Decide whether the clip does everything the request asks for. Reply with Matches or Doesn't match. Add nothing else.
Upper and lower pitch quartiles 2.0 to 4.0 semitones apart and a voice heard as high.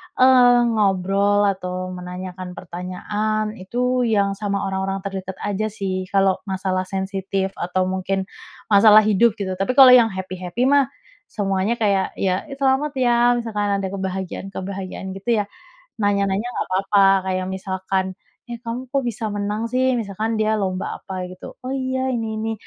Matches